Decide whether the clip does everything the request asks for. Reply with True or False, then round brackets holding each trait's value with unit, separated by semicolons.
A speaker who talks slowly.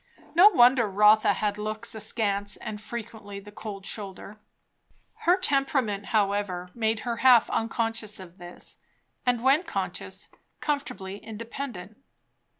True (120 wpm)